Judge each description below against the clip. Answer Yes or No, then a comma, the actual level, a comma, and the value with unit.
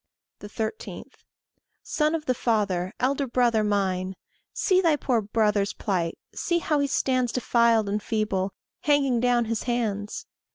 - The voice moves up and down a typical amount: Yes, average, 4.4 semitones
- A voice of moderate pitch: No, high, 230 Hz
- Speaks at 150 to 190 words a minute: No, slow, 135 wpm